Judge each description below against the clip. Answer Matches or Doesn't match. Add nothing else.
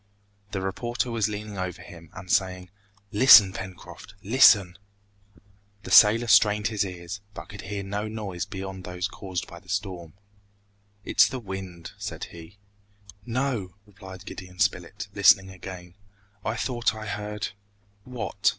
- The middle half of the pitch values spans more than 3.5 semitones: Doesn't match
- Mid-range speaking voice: Doesn't match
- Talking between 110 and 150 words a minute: Matches